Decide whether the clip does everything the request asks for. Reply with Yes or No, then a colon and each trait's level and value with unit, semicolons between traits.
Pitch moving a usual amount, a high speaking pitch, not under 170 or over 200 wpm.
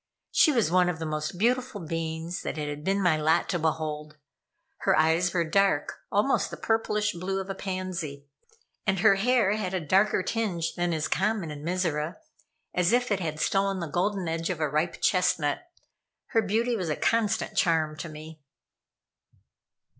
No: average, 3.9 semitones; medium, 180 Hz; average, 175 wpm